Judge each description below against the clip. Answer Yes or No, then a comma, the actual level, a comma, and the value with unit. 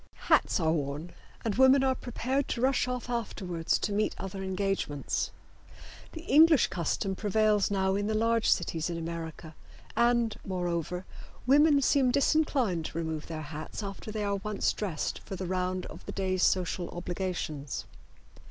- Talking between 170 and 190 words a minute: No, average, 155 wpm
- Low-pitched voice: No, high, 195 Hz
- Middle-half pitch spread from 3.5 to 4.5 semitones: No, wide, 5.6 semitones